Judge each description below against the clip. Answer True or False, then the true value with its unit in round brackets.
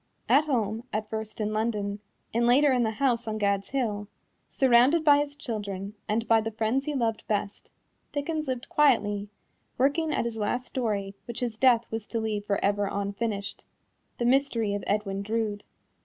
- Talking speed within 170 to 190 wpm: True (175 wpm)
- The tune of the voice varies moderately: True (3.6 semitones)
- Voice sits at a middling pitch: False (225 Hz)